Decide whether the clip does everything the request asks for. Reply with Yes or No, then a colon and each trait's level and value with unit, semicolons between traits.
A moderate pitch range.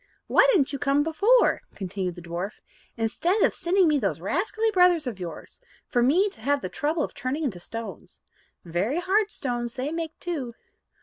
No: wide, 7.4 semitones